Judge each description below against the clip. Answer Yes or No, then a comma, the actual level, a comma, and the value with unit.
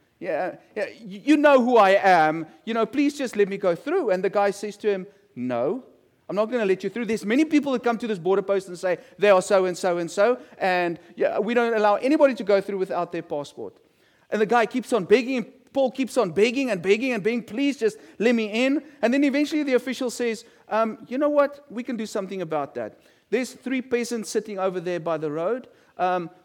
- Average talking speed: No, fast, 235 wpm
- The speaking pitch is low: No, high, 220 Hz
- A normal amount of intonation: Yes, average, 4.8 semitones